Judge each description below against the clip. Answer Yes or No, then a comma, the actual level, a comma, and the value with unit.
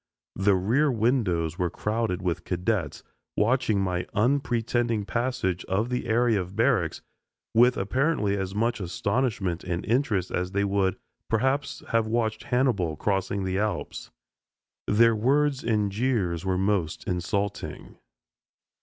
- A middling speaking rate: No, slow, 130 wpm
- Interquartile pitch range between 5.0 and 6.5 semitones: No, average, 4.3 semitones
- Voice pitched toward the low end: Yes, low, 105 Hz